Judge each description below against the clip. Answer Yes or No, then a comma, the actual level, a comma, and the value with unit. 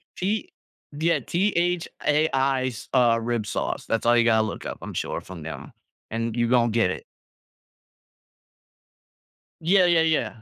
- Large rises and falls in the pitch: Yes, wide, 6.2 semitones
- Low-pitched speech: Yes, low, 125 Hz